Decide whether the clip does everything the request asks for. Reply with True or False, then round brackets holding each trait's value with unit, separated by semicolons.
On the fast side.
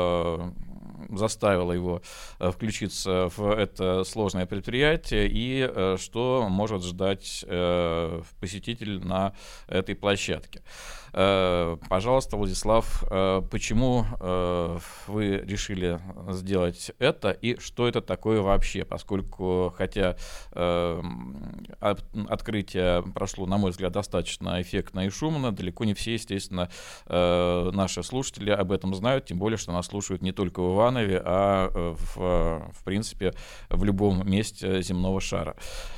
False (110 wpm)